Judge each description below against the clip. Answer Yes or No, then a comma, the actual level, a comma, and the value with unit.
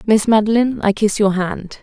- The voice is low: No, high, 210 Hz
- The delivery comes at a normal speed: Yes, average, 195 wpm